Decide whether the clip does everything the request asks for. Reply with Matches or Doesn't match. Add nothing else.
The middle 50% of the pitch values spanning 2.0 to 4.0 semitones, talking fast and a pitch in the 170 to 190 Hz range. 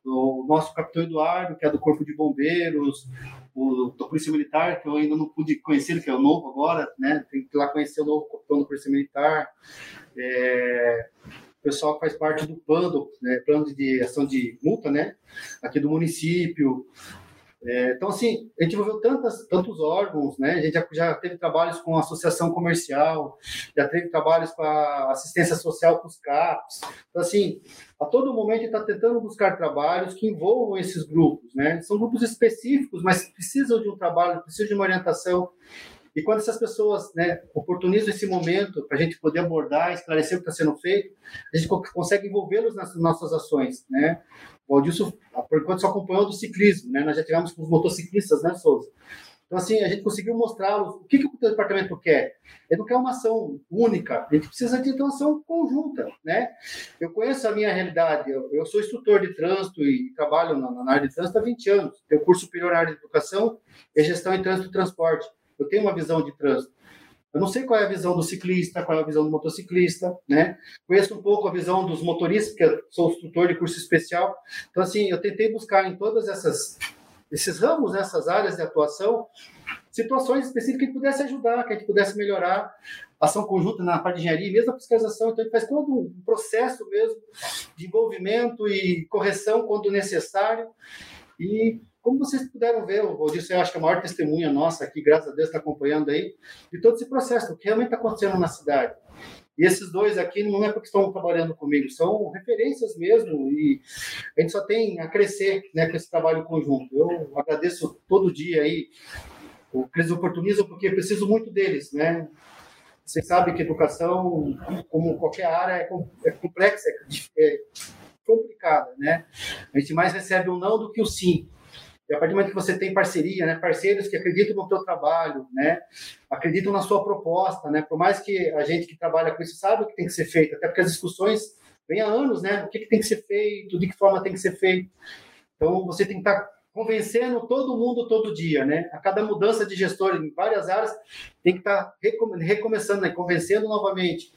Doesn't match